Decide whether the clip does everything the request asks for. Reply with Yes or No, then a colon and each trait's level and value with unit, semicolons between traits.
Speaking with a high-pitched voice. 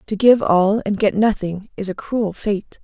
Yes: high, 205 Hz